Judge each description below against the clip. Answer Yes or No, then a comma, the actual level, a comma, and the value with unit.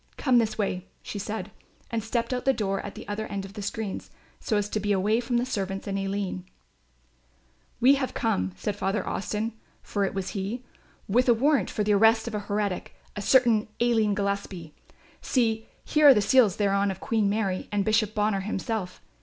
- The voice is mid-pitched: No, high, 210 Hz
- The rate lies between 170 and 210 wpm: Yes, average, 200 wpm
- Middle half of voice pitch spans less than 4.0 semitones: Yes, narrow, 2.4 semitones